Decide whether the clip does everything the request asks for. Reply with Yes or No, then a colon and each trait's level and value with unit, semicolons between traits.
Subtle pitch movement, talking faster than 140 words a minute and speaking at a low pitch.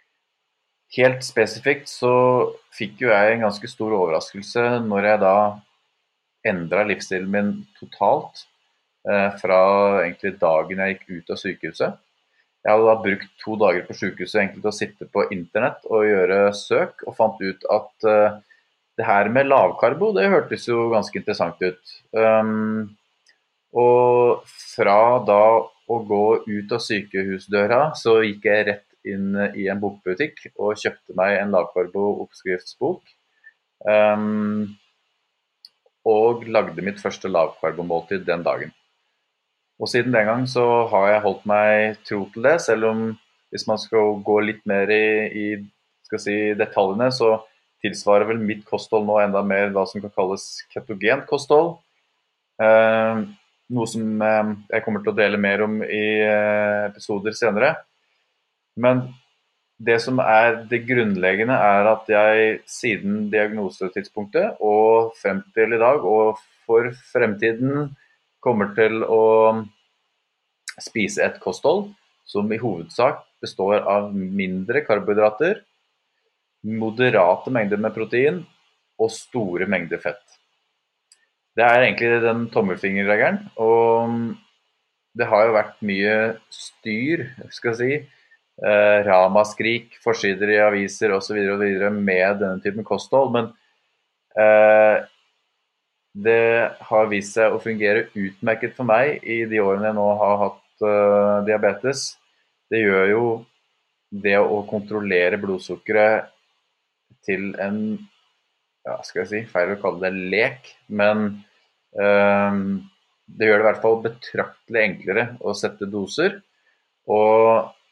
No: narrow, 1.9 semitones; slow, 135 wpm; low, 105 Hz